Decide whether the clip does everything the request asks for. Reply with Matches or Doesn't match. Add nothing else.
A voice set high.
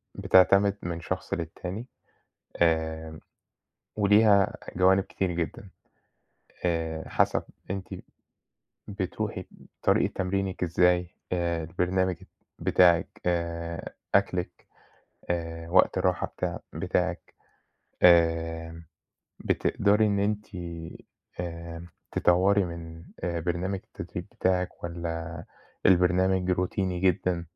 Doesn't match